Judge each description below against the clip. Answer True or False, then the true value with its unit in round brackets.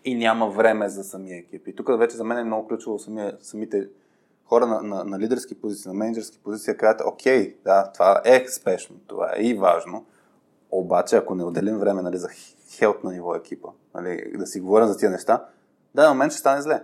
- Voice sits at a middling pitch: False (105 Hz)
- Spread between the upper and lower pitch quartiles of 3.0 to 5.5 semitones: False (2.6 semitones)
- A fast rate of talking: True (210 wpm)